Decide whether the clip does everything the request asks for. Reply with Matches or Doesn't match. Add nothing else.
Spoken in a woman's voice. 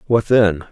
Doesn't match